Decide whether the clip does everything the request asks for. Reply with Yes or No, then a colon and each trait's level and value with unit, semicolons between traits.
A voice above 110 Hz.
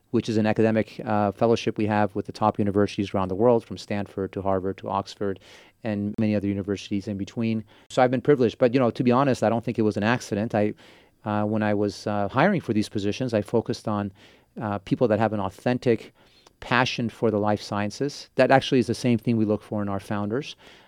No: low, 105 Hz